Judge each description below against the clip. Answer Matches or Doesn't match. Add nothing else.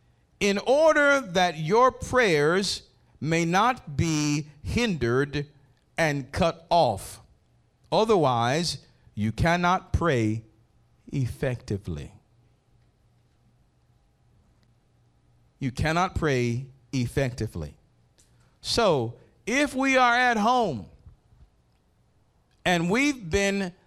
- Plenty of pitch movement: Matches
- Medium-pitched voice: Matches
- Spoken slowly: Matches